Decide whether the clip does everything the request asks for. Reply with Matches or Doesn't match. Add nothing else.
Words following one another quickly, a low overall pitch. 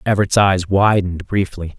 Doesn't match